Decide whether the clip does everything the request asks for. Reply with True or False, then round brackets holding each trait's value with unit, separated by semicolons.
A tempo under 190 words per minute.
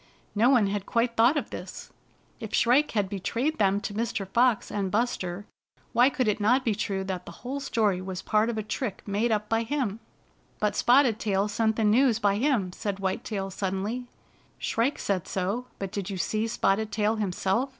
False (200 wpm)